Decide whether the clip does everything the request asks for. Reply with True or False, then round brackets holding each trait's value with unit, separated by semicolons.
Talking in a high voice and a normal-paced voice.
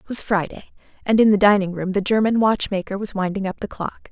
False (200 Hz; 235 wpm)